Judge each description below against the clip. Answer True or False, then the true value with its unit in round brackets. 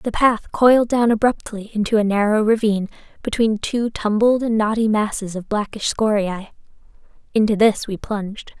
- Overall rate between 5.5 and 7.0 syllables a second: False (5.0 syllables/s)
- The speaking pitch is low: False (215 Hz)